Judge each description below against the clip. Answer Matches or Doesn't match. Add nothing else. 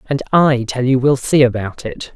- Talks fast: Matches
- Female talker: Doesn't match